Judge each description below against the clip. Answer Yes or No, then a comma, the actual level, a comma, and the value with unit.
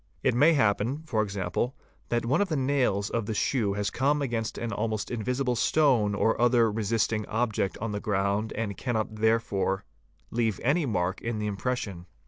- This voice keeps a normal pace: Yes, average, 175 wpm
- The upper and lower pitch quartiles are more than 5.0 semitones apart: No, average, 3.3 semitones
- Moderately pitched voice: No, low, 110 Hz